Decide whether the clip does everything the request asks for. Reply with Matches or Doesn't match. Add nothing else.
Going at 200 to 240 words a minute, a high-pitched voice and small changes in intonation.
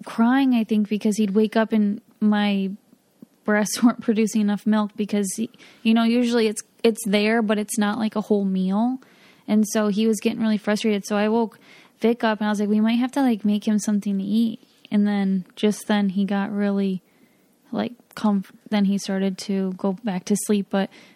Matches